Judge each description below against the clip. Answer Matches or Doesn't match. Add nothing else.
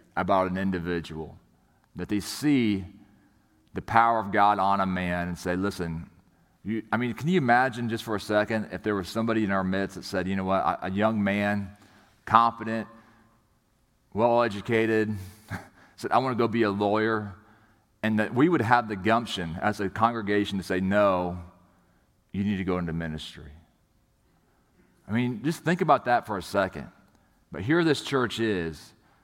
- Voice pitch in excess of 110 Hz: Doesn't match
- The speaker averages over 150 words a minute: Matches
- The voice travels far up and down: Doesn't match